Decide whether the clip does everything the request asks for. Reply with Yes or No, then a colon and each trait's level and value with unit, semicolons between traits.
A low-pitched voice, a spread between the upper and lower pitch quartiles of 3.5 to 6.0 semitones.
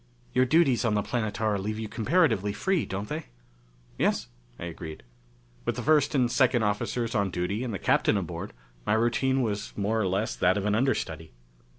Yes: low, 110 Hz; average, 4.0 semitones